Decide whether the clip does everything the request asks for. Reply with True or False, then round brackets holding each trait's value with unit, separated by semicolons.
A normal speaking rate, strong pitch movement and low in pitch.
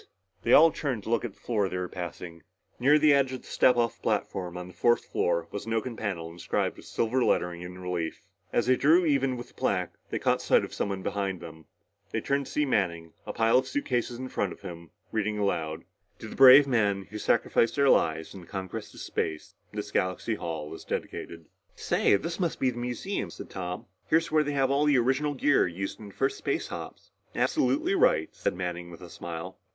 False (220 wpm; 7.1 semitones; 105 Hz)